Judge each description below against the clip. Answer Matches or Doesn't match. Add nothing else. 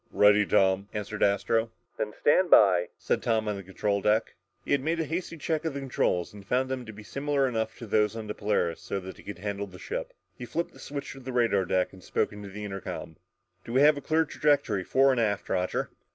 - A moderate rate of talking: Doesn't match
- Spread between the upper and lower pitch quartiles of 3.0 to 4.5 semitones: Doesn't match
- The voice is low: Matches